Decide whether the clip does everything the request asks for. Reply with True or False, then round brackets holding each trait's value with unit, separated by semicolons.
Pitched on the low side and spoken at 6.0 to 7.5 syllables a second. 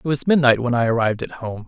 True (125 Hz; 6.8 syllables/s)